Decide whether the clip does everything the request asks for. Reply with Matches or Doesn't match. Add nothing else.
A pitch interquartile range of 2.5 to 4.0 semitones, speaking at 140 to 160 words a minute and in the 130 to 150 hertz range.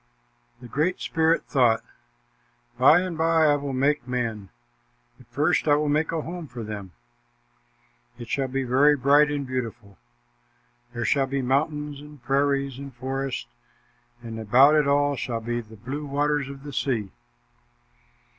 Matches